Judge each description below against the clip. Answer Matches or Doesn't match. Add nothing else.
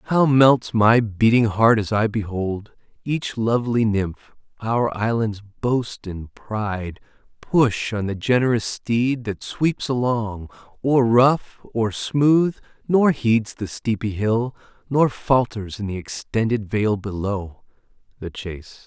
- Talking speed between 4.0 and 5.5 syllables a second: Doesn't match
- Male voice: Matches